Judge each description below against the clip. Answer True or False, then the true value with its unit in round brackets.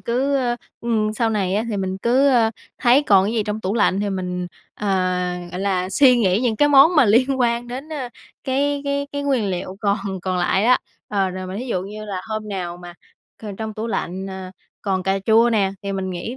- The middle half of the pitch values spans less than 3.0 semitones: False (4.3 semitones)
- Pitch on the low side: False (215 Hz)